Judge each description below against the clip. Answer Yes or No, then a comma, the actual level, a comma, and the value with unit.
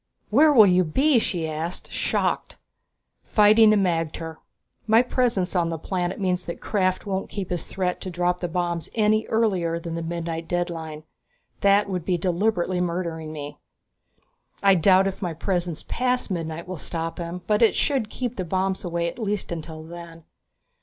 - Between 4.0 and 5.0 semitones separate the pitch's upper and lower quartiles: No, average, 3.2 semitones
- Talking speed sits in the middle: Yes, average, 170 wpm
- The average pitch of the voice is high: No, medium, 180 Hz